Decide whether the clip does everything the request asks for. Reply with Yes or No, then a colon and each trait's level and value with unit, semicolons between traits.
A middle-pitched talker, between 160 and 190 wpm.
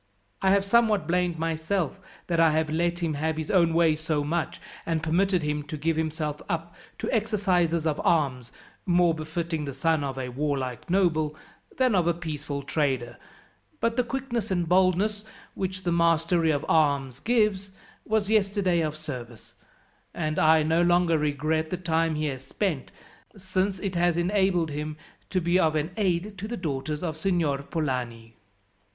Yes: medium, 165 Hz; average, 165 wpm